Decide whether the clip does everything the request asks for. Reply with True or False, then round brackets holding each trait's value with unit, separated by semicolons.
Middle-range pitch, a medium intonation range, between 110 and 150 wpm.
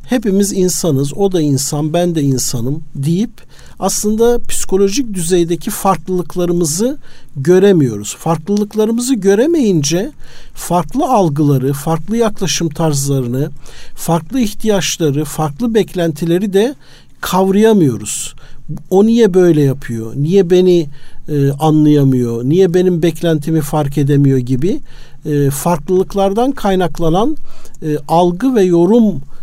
False (175 Hz; 5.0 semitones; 100 wpm)